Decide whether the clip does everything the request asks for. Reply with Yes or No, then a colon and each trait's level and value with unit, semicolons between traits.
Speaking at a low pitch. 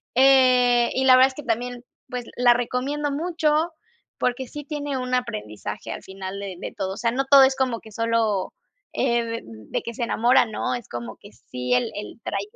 No: high, 245 Hz